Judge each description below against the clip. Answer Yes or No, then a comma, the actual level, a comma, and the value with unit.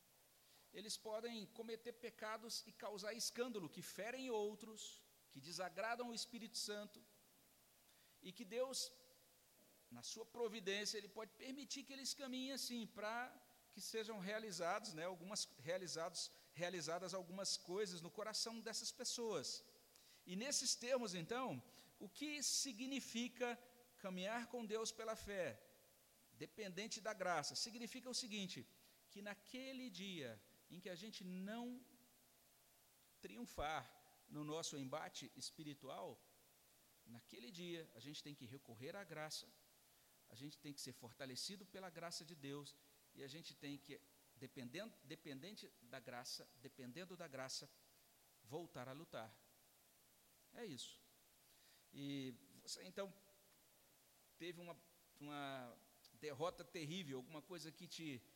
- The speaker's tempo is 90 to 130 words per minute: Yes, average, 125 wpm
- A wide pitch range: Yes, wide, 7.4 semitones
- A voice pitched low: No, high, 190 Hz